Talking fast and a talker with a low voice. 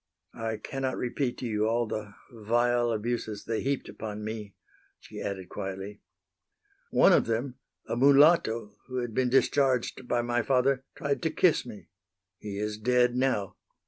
No: average, 155 wpm; low, 120 Hz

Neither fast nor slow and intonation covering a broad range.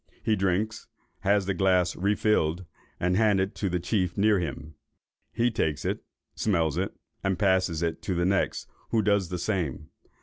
No: average, 165 wpm; average, 2.8 semitones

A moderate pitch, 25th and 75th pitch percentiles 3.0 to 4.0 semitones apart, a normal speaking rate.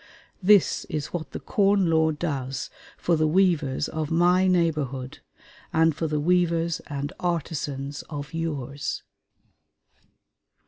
No: medium, 160 Hz; average, 3.3 semitones; slow, 120 wpm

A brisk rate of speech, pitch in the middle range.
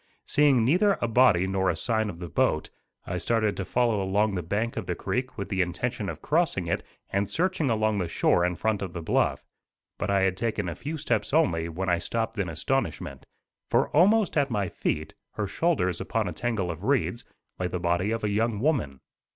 No: fast, 210 wpm; low, 105 Hz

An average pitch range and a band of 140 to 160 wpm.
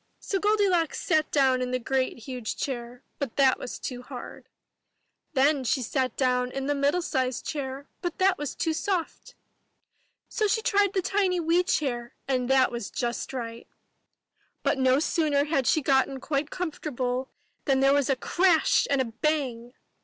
No: average, 4.2 semitones; average, 170 wpm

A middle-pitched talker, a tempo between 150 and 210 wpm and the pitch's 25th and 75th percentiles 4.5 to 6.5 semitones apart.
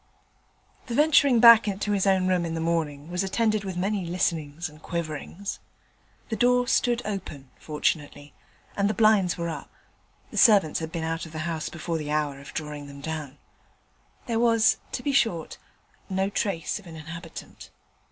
Yes: medium, 175 Hz; average, 170 wpm; average, 5.1 semitones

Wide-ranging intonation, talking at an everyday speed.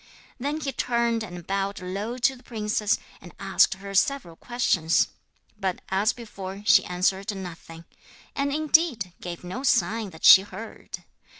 No: average, 4.5 semitones; average, 145 wpm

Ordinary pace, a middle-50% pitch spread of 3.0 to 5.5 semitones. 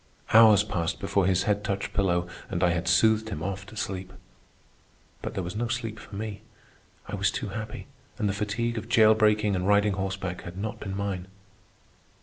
No: average, 190 wpm; narrow, 2.4 semitones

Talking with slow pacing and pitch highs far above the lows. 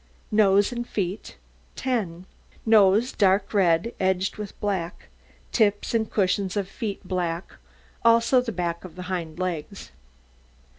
No: slow, 130 wpm; average, 3.1 semitones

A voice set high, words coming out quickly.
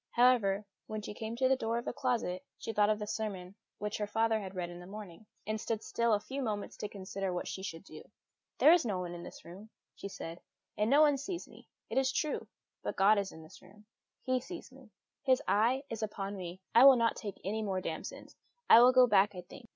Yes: high, 215 Hz; fast, 235 wpm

